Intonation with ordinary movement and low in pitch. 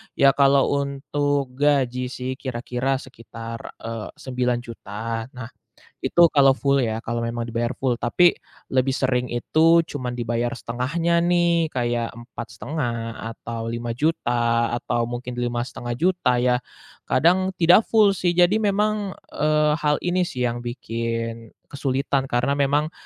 Yes: average, 3.8 semitones; low, 125 Hz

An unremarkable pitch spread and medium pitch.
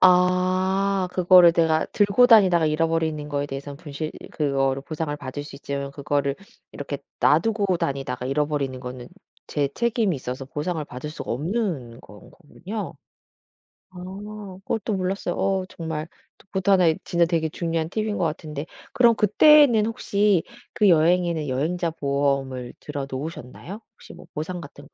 Yes: average, 4.7 semitones; medium, 160 Hz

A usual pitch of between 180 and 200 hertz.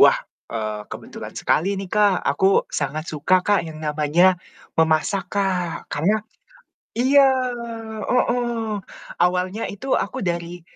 Yes: medium, 185 Hz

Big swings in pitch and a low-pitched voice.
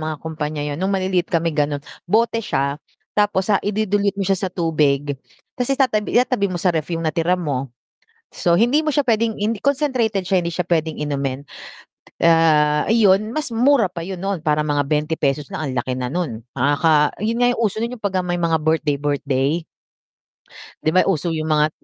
No: wide, 5.7 semitones; medium, 170 Hz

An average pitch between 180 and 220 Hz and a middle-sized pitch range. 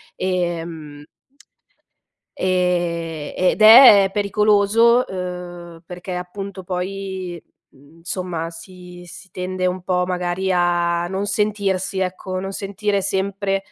No: medium, 185 Hz; narrow, 1.9 semitones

